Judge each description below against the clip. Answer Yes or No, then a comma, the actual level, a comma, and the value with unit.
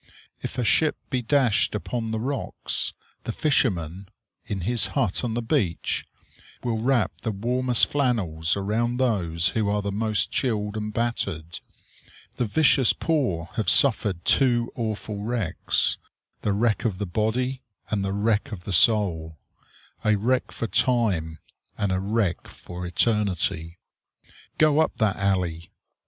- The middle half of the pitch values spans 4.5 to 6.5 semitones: No, average, 4.0 semitones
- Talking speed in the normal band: Yes, average, 145 wpm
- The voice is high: No, low, 110 Hz